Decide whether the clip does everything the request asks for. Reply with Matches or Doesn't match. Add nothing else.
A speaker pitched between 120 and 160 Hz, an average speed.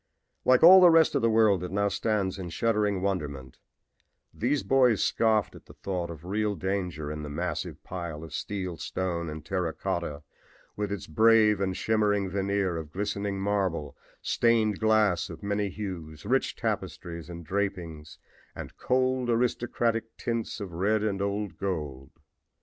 Doesn't match